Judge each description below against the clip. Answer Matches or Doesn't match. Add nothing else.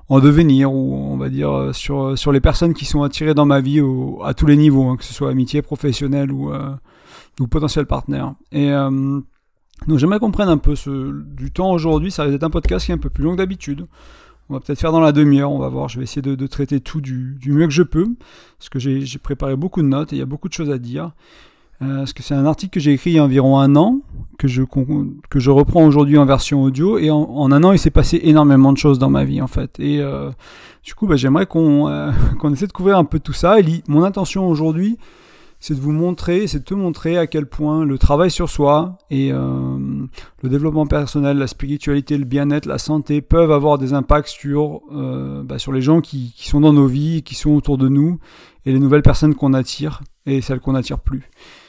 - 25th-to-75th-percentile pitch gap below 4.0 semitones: Matches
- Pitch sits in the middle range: Matches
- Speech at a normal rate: Doesn't match